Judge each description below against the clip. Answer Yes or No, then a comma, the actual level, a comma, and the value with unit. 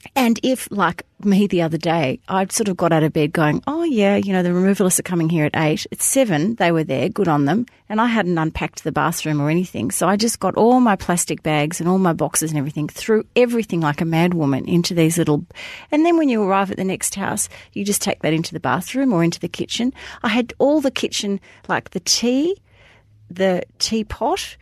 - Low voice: No, medium, 185 Hz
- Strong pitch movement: Yes, wide, 5.8 semitones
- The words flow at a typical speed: No, fast, 230 wpm